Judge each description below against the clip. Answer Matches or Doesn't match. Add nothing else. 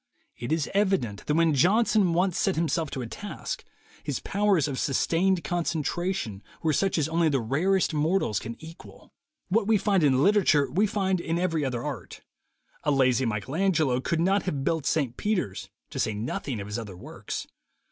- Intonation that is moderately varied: Doesn't match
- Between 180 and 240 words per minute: Matches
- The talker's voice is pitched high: Doesn't match